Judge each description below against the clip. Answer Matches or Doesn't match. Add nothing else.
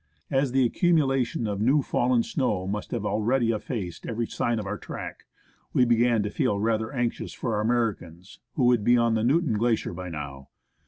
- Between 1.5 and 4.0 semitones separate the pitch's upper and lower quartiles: Matches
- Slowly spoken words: Doesn't match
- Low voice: Matches